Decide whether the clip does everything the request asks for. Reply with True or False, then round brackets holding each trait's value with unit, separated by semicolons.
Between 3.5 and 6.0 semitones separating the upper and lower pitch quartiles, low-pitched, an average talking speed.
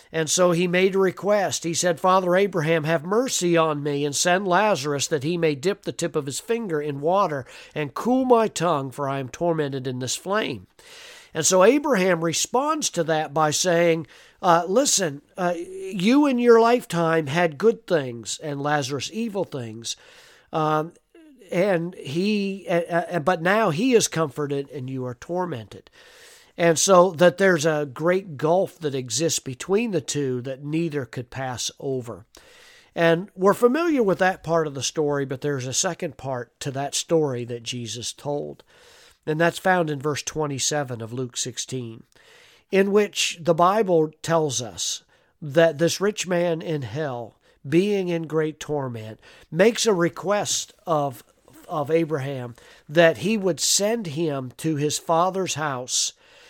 False (4.7 semitones; 165 Hz; 160 wpm)